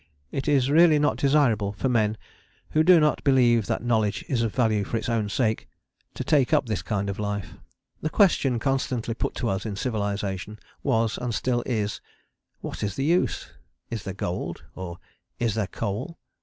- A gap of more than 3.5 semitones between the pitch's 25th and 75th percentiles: Yes, average, 4.7 semitones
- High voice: No, low, 115 Hz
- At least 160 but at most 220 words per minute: Yes, average, 185 wpm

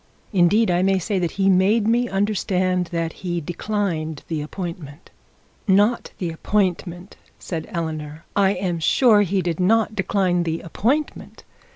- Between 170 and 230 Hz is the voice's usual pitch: Yes, medium, 185 Hz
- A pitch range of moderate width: Yes, average, 3.4 semitones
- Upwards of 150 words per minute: No, average, 145 wpm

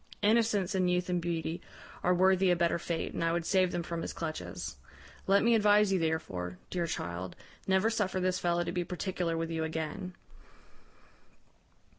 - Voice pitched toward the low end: No, medium, 175 Hz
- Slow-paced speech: No, average, 175 wpm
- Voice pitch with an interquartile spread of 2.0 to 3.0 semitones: Yes, narrow, 2.4 semitones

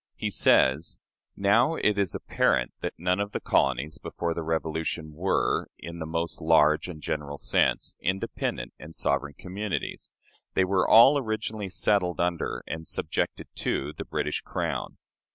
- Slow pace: No, average, 150 wpm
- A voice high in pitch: No, very low, 85 Hz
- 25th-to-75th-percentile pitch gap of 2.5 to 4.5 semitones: Yes, average, 4.2 semitones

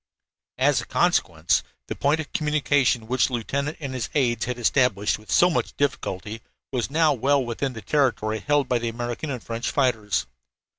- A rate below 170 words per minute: No, average, 180 wpm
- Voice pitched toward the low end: Yes, low, 125 Hz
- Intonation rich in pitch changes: No, average, 3.8 semitones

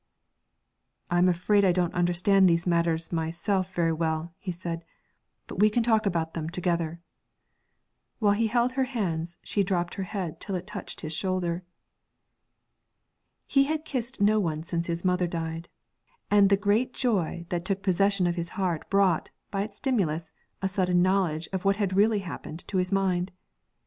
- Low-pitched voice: No, medium, 185 Hz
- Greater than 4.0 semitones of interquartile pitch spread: No, average, 3.0 semitones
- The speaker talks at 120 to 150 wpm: No, average, 170 wpm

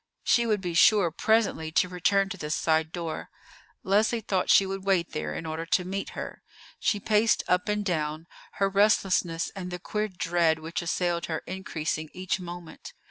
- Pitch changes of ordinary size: Yes, average, 3.1 semitones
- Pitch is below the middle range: No, medium, 180 Hz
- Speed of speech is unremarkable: Yes, average, 180 wpm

